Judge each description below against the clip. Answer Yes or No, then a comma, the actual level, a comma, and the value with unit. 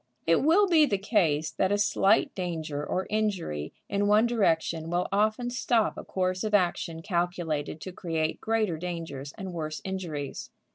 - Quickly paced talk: No, average, 160 wpm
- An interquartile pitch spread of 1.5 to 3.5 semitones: No, average, 4.4 semitones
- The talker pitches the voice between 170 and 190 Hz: Yes, medium, 185 Hz